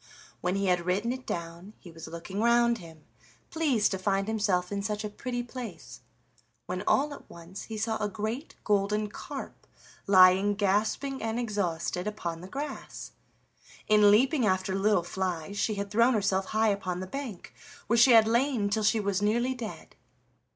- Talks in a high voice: Yes, high, 205 Hz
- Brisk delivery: No, average, 170 wpm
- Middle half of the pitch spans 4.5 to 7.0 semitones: No, average, 3.5 semitones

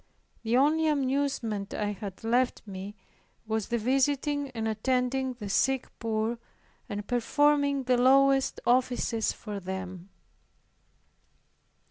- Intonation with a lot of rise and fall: No, average, 4.0 semitones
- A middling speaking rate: No, slow, 110 wpm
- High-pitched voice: Yes, high, 245 Hz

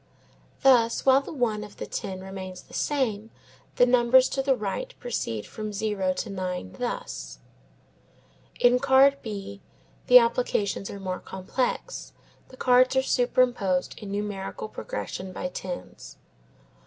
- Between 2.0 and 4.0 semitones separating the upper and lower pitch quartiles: No, average, 4.8 semitones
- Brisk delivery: No, slow, 135 wpm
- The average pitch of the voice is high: Yes, high, 220 Hz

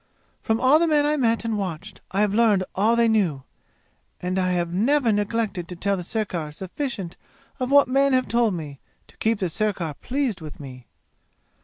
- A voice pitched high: Yes, high, 210 Hz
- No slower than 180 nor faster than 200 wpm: Yes, average, 190 wpm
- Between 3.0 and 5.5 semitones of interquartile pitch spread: Yes, average, 4.9 semitones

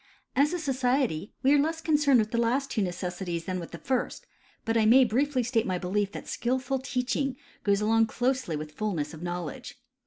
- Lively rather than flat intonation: Yes, wide, 6.2 semitones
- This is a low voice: No, high, 235 Hz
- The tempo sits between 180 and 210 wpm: Yes, average, 195 wpm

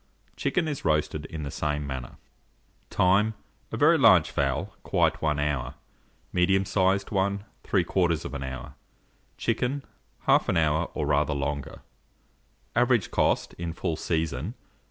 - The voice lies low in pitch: Yes, very low, 80 Hz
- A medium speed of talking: No, slow, 130 wpm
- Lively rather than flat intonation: No, average, 5.0 semitones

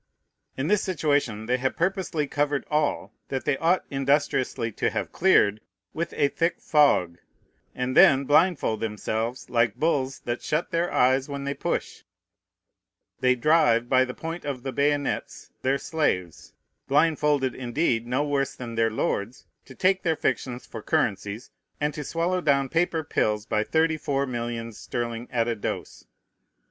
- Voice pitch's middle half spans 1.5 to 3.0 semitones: No, average, 4.3 semitones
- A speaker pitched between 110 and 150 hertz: Yes, low, 135 Hz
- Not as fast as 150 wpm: No, average, 155 wpm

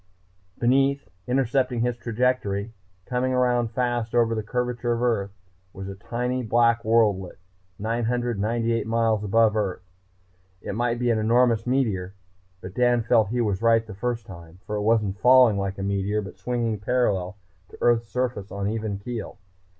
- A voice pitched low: Yes, low, 115 Hz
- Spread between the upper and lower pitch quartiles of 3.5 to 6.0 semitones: No, average, 2.9 semitones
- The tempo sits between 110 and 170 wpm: Yes, average, 160 wpm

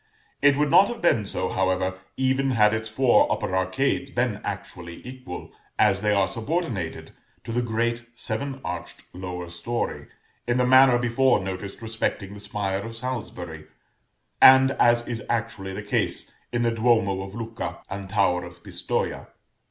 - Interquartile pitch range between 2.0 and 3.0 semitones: No, average, 4.4 semitones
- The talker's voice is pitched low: Yes, low, 110 Hz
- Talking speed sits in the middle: Yes, average, 160 wpm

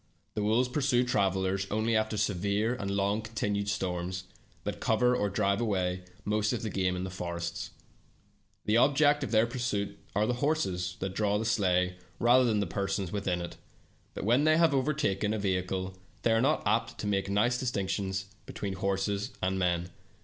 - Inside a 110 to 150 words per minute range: No, average, 180 wpm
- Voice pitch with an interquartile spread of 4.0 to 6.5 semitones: No, average, 3.4 semitones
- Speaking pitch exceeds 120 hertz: No, low, 105 Hz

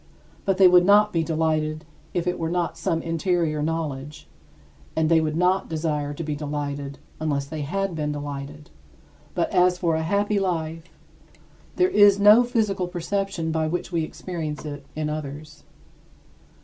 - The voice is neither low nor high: Yes, medium, 160 Hz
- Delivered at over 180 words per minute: No, average, 160 wpm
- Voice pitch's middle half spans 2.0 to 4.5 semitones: Yes, average, 3.1 semitones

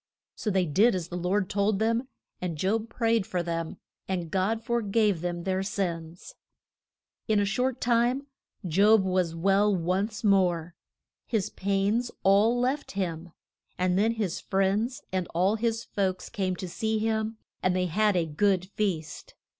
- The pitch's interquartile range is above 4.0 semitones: No, average, 3.4 semitones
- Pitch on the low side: No, high, 195 Hz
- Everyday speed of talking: Yes, average, 160 wpm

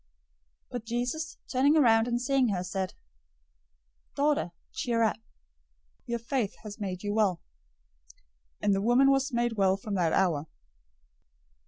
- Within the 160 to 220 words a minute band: No, average, 140 wpm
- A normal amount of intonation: Yes, average, 4.5 semitones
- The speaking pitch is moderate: No, high, 225 Hz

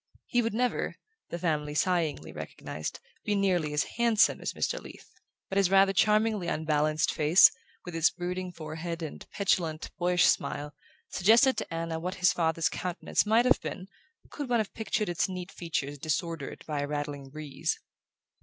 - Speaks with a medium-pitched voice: Yes, medium, 175 Hz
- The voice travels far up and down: No, average, 4.3 semitones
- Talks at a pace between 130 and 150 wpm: No, average, 165 wpm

